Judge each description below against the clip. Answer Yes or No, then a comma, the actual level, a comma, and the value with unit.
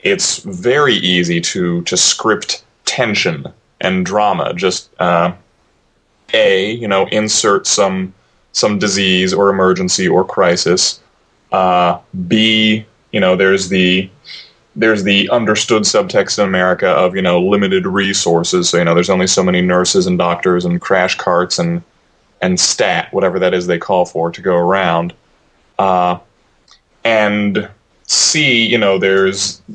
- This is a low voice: Yes, very low, 95 Hz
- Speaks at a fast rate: No, average, 140 wpm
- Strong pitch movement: No, narrow, 2.5 semitones